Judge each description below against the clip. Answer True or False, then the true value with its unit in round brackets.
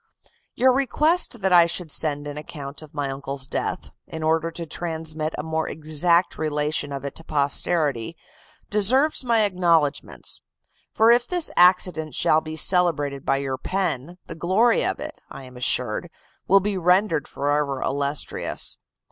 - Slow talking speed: False (155 wpm)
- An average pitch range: True (4.1 semitones)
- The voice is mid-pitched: True (160 Hz)